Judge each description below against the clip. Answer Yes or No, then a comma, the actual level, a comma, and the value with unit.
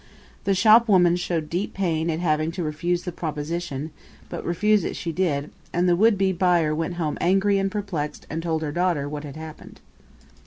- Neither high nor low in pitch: Yes, medium, 175 Hz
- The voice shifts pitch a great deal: No, average, 3.1 semitones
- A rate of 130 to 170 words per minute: No, average, 190 wpm